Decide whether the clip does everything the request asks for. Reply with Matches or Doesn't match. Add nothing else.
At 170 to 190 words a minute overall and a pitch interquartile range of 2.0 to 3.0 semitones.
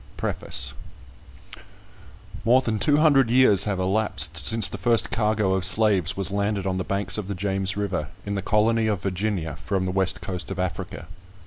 Matches